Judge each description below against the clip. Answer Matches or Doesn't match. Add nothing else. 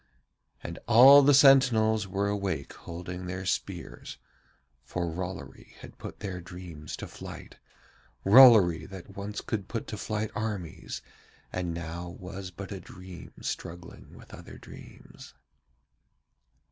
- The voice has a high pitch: Doesn't match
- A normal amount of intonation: Matches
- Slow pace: Matches